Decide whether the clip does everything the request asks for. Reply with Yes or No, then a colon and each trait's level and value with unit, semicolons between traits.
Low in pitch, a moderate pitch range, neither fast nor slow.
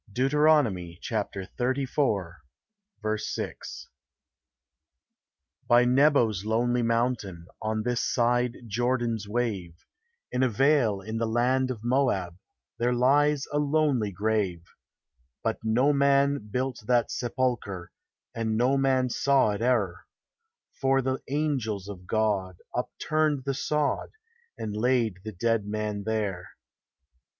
No: low, 120 Hz; average, 4.1 semitones; slow, 110 wpm